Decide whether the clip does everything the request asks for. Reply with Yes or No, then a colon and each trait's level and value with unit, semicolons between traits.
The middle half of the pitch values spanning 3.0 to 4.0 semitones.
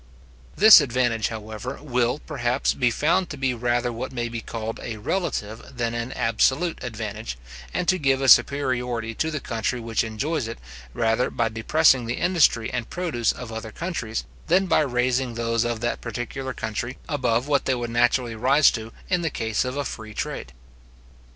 Yes: average, 3.3 semitones